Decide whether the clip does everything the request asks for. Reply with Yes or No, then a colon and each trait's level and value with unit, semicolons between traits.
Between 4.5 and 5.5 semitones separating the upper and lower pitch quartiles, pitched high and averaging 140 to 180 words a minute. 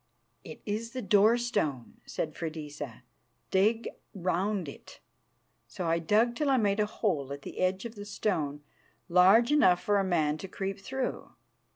Yes: average, 5.0 semitones; high, 195 Hz; average, 165 wpm